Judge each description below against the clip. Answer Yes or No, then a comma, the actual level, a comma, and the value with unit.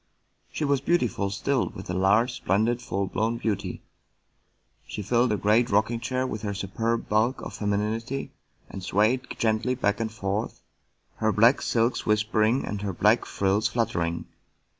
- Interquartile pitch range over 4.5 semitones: No, average, 2.8 semitones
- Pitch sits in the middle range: No, low, 110 Hz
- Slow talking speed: No, average, 155 wpm